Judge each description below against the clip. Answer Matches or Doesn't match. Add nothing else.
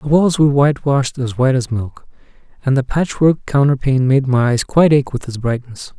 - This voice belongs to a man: Matches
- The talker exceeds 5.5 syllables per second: Matches